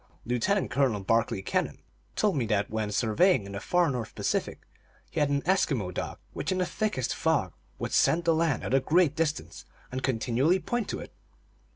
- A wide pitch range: Yes, wide, 7.3 semitones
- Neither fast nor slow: Yes, average, 190 wpm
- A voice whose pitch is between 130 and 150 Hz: Yes, low, 135 Hz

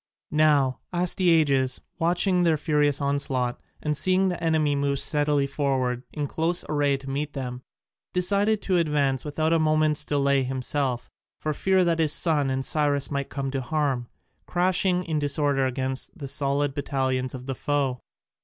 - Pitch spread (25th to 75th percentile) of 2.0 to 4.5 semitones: Yes, average, 2.9 semitones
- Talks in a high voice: No, medium, 145 Hz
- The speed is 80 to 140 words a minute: No, average, 155 wpm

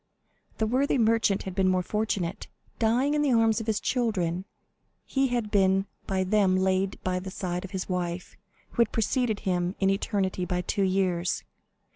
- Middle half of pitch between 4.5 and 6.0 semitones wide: No, average, 3.2 semitones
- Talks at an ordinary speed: Yes, average, 175 wpm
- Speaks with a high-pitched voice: Yes, high, 195 Hz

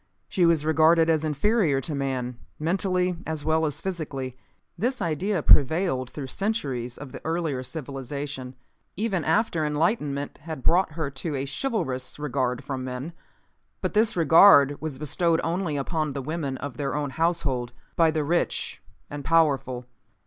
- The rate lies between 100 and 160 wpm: Yes, average, 150 wpm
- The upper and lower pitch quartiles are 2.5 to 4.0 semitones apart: Yes, average, 3.7 semitones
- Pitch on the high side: No, medium, 150 Hz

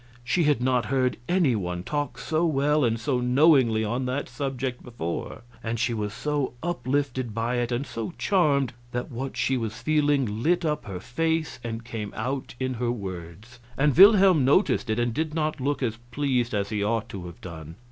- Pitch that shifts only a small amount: No, average, 4.3 semitones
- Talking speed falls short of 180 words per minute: No, average, 190 wpm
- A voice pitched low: Yes, low, 125 Hz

